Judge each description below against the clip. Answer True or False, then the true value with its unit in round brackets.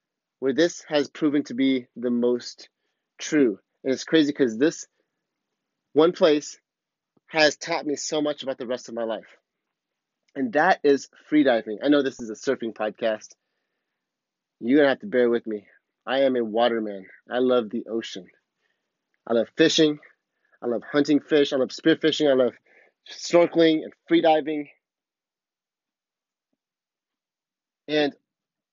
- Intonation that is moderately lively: True (4.4 semitones)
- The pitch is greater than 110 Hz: True (135 Hz)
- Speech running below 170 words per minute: True (145 wpm)